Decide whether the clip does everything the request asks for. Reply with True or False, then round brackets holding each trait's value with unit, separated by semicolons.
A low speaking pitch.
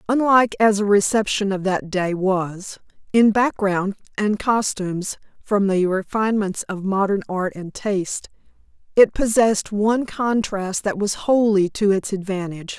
False (200 Hz)